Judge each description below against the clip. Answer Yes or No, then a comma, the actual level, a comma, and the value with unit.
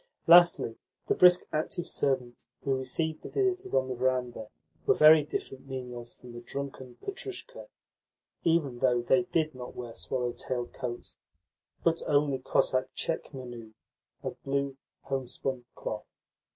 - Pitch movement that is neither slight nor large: Yes, average, 4.0 semitones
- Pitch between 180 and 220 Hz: No, low, 130 Hz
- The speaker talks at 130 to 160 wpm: Yes, slow, 135 wpm